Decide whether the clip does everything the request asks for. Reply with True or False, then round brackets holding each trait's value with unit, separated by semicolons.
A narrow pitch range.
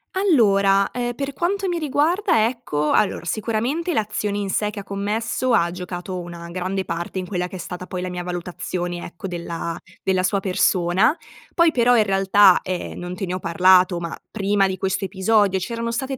False (4.3 semitones)